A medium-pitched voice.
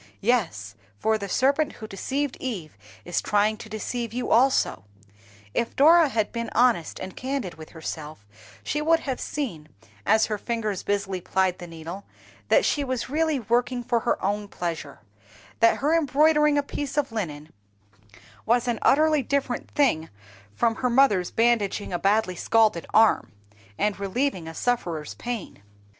No: high, 225 Hz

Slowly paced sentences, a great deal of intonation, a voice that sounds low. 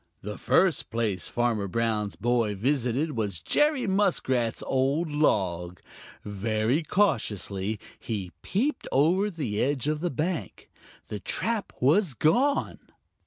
Yes: slow, 120 wpm; wide, 7.9 semitones; low, 125 Hz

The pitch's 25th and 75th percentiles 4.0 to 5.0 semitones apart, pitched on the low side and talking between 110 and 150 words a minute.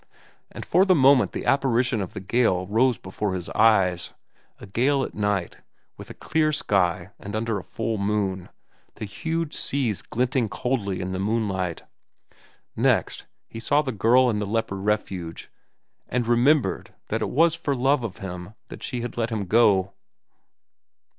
No: average, 4.7 semitones; low, 110 Hz; average, 160 wpm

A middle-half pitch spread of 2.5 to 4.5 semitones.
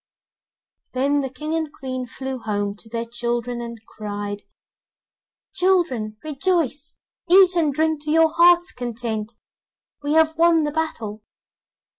No: wide, 5.5 semitones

